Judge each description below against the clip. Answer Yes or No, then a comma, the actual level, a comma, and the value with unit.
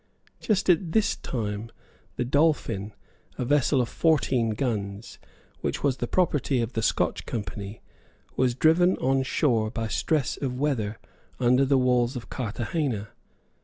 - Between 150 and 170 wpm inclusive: No, average, 140 wpm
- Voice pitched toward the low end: Yes, low, 125 Hz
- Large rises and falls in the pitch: No, average, 4.4 semitones